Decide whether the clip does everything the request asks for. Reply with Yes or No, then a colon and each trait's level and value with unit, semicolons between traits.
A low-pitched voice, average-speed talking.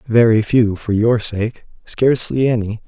Yes: low, 115 Hz; average, 145 wpm